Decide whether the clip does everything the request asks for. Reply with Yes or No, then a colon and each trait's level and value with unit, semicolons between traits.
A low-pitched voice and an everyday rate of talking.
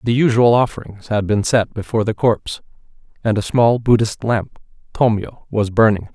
Yes: low, 110 Hz; average, 145 wpm